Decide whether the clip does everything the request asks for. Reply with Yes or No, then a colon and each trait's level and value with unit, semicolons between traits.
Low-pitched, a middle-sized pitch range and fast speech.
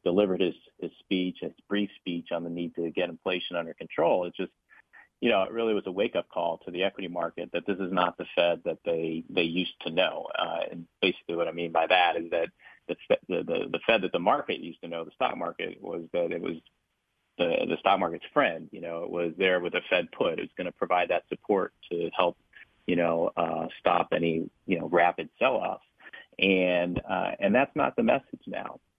No: very low, 85 Hz; narrow, 1.6 semitones; fast, 230 wpm